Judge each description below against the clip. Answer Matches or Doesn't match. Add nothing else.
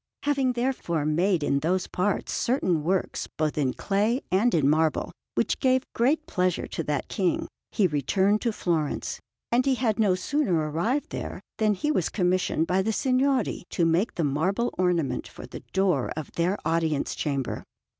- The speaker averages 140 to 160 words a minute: Doesn't match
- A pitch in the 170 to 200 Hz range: Matches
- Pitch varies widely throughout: Matches